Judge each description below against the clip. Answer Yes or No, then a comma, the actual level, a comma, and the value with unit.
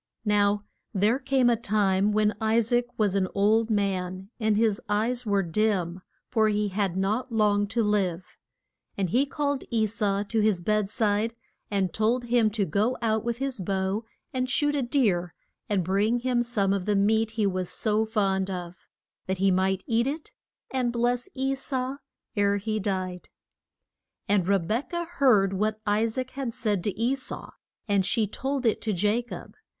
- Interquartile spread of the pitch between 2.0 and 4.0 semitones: Yes, average, 3.3 semitones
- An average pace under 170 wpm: No, average, 180 wpm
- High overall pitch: Yes, high, 215 Hz